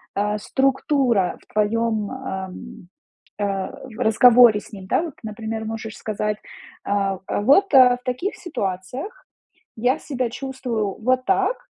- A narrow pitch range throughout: No, average, 3.9 semitones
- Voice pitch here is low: No, high, 225 Hz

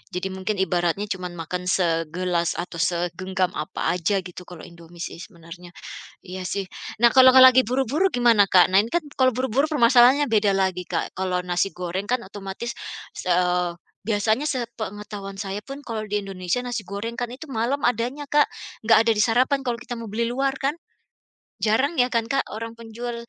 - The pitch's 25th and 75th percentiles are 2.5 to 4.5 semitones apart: No, average, 5.2 semitones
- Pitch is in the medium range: No, high, 210 Hz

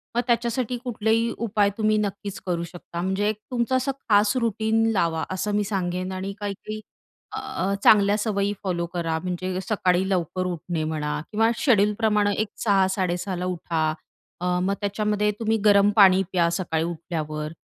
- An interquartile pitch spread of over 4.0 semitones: No, average, 3.1 semitones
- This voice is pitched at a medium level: No, high, 195 Hz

